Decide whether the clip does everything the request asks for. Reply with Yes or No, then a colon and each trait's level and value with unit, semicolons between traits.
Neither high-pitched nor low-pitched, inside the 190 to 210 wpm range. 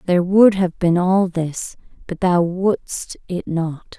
No: medium, 180 Hz; average, 150 wpm